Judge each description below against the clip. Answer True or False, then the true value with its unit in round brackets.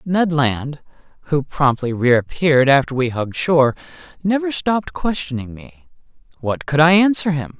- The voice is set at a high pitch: False (150 Hz)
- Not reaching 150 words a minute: True (140 wpm)